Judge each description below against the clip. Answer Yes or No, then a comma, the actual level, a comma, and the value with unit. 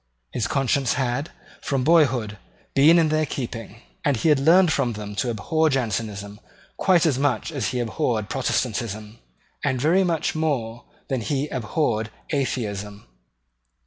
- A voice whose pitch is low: Yes, low, 130 Hz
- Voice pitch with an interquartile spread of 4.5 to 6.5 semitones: Yes, average, 5.3 semitones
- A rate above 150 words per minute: No, average, 145 wpm